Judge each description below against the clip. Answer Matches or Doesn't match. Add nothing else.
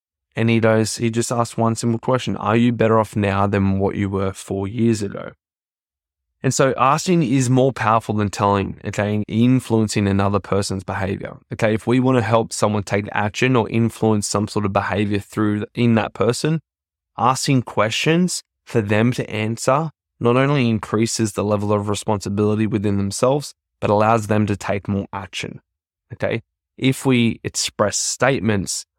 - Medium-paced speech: Matches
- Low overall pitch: Matches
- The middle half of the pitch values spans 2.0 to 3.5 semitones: Matches